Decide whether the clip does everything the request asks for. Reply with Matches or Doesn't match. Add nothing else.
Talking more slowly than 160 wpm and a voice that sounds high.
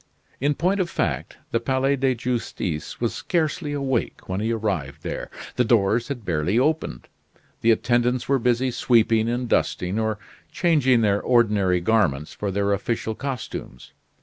Doesn't match